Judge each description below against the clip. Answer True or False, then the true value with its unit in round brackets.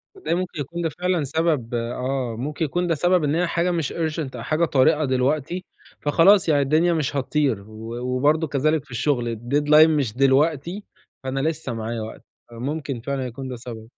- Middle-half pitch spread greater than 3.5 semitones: True (4.1 semitones)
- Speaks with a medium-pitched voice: True (145 Hz)